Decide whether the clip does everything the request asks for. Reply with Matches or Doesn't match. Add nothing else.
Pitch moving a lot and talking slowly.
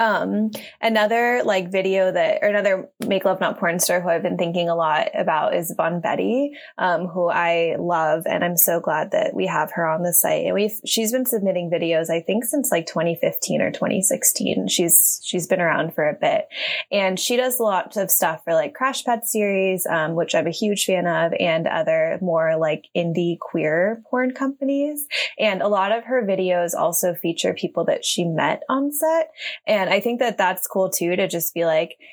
Doesn't match